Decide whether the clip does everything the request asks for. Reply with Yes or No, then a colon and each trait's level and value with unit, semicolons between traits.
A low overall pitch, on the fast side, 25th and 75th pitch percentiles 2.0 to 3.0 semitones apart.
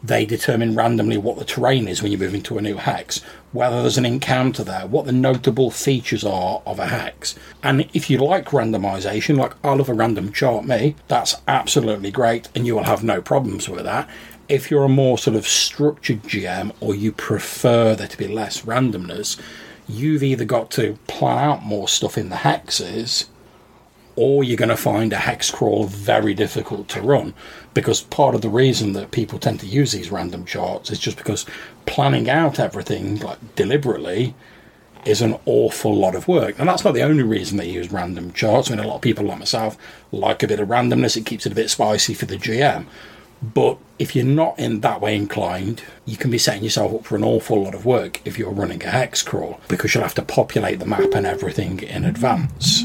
No: low, 115 Hz; fast, 210 wpm; average, 4.1 semitones